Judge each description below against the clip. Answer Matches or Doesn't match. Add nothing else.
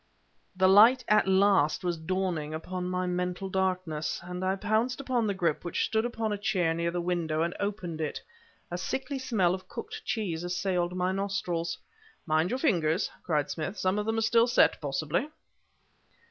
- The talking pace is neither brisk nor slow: Matches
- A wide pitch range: Doesn't match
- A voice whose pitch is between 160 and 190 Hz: Matches